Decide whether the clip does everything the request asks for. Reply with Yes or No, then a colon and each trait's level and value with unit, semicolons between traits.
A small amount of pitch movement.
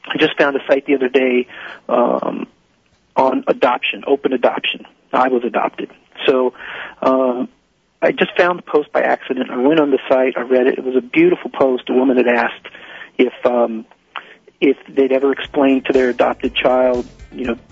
Yes: narrow, 1.8 semitones